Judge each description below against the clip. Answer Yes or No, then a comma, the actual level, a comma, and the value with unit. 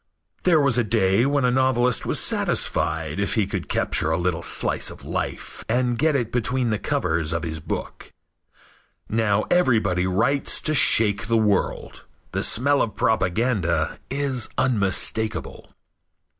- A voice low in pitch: Yes, low, 110 Hz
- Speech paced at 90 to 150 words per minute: Yes, average, 145 wpm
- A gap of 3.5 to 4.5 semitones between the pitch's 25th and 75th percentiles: No, average, 5.2 semitones